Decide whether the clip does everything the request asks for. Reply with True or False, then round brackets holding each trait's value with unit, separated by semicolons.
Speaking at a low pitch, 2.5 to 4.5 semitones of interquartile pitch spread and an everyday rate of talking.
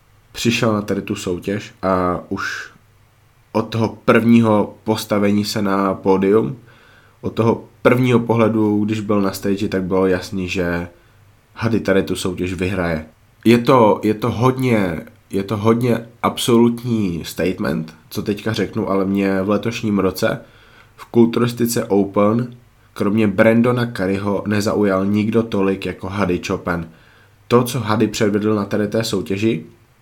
True (105 Hz; 2.8 semitones; 140 wpm)